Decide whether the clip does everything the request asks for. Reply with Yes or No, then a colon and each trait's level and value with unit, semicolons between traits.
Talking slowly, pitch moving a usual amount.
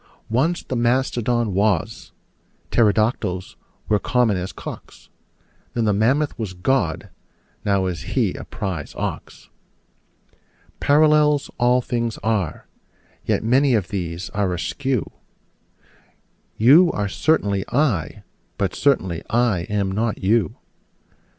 Yes: slow, 110 wpm; average, 4.7 semitones